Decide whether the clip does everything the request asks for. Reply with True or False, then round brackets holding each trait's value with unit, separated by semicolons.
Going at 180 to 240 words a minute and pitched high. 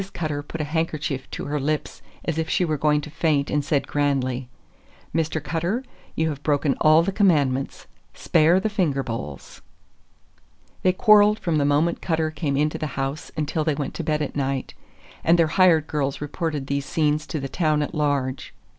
False (185 wpm; 150 Hz)